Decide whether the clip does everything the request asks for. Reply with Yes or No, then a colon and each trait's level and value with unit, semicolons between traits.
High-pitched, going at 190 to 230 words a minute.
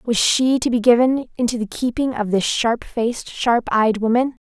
Yes: high, 235 Hz; average, 200 wpm